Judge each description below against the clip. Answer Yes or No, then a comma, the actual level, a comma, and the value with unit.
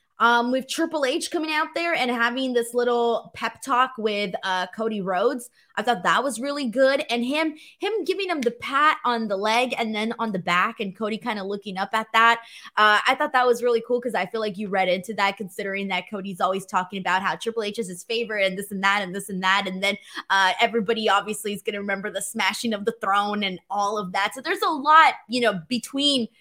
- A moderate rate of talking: No, fast, 240 wpm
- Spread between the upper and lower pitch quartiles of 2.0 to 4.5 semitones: Yes, average, 3.7 semitones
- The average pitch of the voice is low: No, high, 225 Hz